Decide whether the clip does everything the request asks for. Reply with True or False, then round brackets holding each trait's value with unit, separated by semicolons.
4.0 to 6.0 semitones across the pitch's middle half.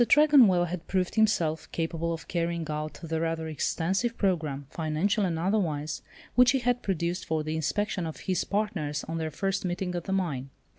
False (3.5 semitones)